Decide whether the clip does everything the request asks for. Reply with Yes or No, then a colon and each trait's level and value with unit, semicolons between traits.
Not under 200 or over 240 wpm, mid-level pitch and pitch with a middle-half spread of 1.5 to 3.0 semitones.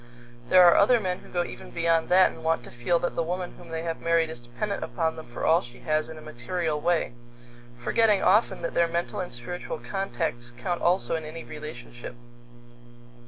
Yes: fast, 205 wpm; medium, 165 Hz; narrow, 2.6 semitones